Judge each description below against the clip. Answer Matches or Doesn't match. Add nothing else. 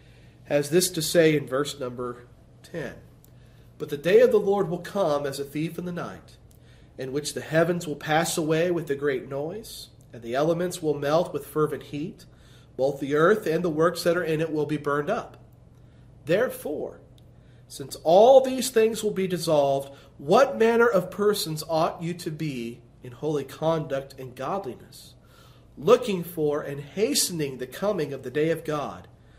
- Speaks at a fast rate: Doesn't match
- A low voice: Doesn't match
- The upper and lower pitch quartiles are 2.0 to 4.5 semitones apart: Matches